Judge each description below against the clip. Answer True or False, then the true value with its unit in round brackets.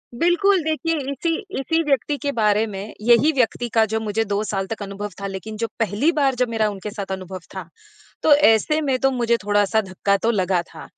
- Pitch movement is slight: False (5.3 semitones)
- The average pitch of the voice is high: True (220 Hz)